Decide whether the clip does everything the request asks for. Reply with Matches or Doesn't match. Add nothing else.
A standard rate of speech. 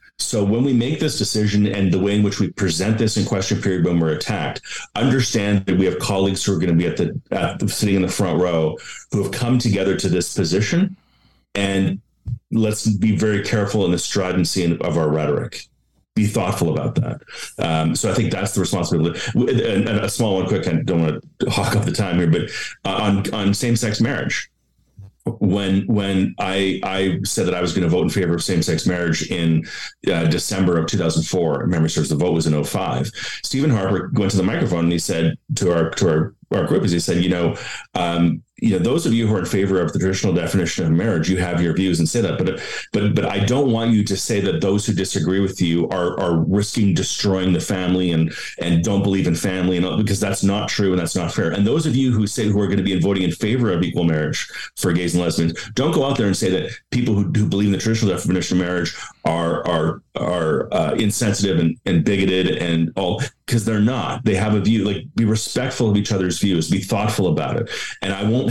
Doesn't match